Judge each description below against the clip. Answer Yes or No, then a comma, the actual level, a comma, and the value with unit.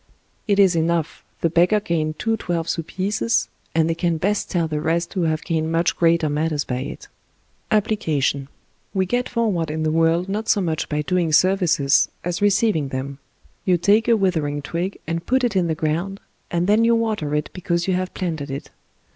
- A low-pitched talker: No, medium, 170 Hz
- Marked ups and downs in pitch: No, average, 3.7 semitones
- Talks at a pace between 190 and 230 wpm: Yes, average, 195 wpm